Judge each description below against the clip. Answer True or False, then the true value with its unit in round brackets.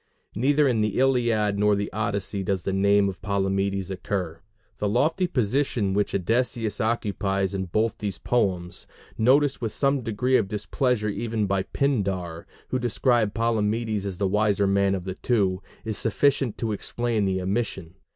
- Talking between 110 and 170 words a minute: True (160 wpm)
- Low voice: True (105 Hz)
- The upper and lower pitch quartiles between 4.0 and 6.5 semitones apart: False (3.4 semitones)